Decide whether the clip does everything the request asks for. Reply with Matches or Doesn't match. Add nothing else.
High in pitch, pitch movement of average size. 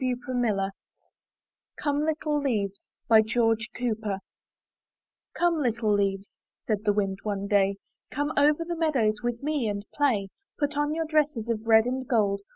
Doesn't match